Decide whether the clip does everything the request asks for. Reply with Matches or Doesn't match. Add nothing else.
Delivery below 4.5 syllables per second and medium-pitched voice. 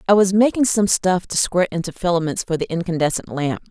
Doesn't match